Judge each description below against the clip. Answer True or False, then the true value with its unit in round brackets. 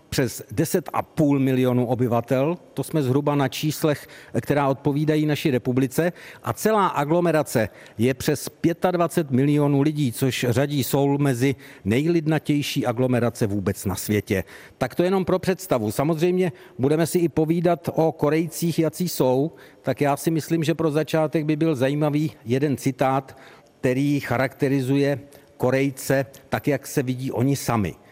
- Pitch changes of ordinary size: True (3.3 semitones)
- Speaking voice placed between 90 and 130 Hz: False (140 Hz)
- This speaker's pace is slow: False (140 wpm)